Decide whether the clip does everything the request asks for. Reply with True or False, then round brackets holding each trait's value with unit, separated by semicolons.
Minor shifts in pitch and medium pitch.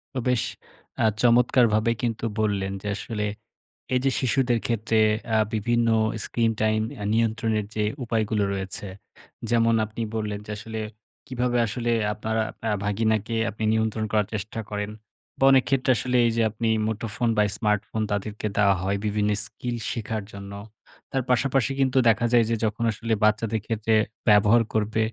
False (1.9 semitones; 110 Hz)